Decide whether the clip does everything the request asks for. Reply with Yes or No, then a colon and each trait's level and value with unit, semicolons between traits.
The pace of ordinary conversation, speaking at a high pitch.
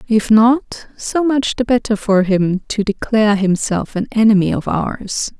Yes: average, 165 wpm; high, 215 Hz